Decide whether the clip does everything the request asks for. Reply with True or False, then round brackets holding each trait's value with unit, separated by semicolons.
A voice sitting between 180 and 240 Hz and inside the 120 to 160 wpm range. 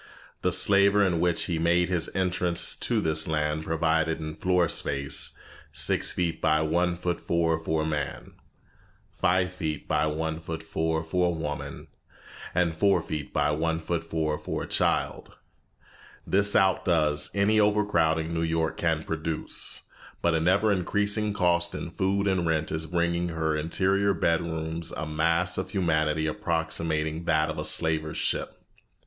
False (80 Hz; 155 wpm)